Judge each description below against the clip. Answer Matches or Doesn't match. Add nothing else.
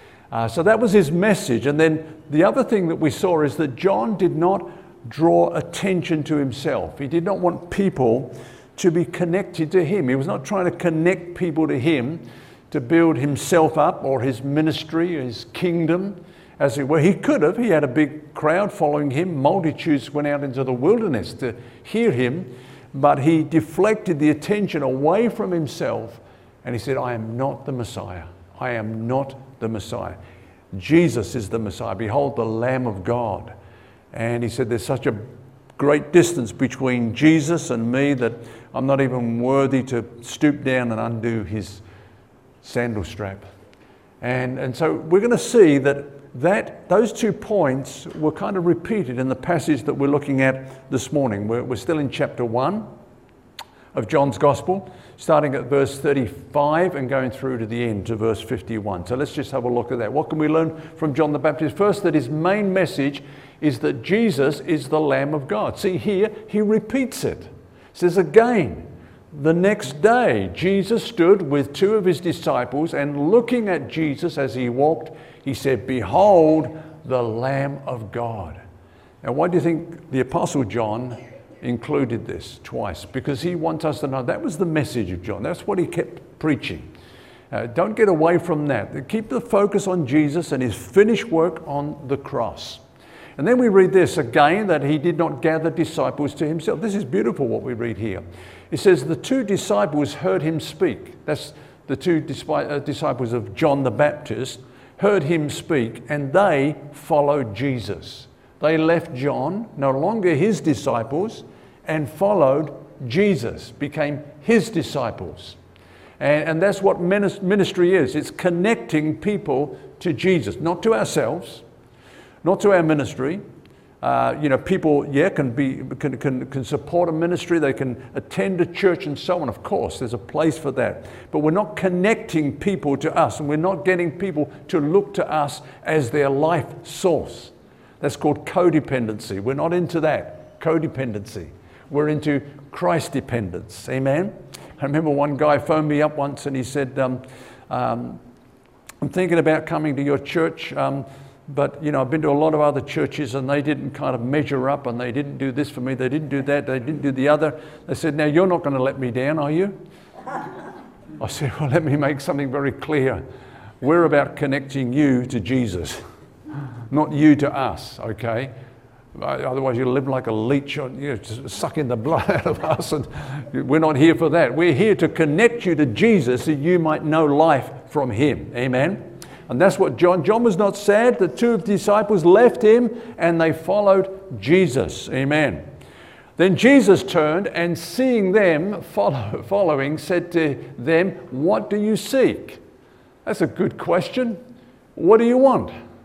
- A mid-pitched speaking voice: Matches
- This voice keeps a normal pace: Matches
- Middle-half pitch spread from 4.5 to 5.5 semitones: Matches